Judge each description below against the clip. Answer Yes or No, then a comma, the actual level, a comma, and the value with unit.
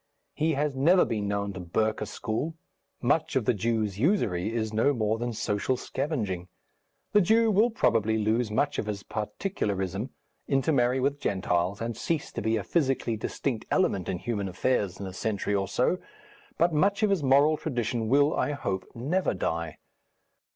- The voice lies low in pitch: Yes, low, 115 Hz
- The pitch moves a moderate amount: No, wide, 6.0 semitones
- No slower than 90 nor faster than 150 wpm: No, average, 170 wpm